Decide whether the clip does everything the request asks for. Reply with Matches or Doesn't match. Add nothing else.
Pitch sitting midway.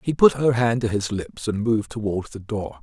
Doesn't match